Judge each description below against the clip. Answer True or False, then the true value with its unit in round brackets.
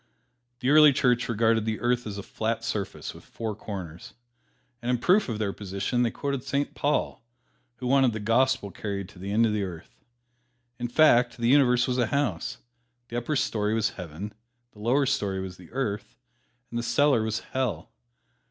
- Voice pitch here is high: False (115 Hz)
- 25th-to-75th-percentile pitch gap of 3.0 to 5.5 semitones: True (3.6 semitones)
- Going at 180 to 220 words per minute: True (185 wpm)